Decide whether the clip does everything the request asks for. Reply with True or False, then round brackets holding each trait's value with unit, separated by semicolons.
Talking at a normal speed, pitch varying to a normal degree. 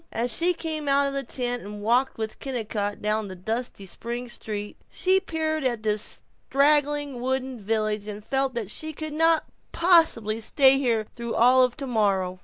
True (175 wpm; 4.7 semitones)